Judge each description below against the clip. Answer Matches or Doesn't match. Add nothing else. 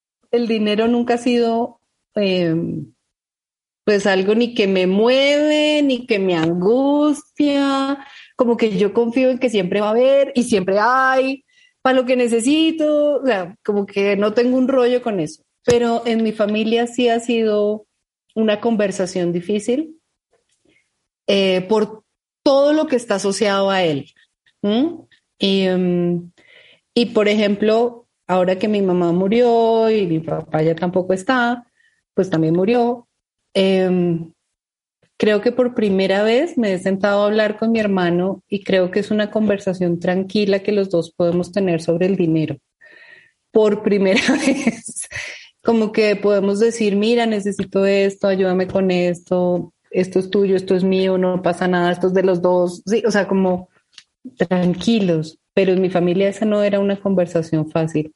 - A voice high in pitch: Matches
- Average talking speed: Matches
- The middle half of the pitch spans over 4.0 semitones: Matches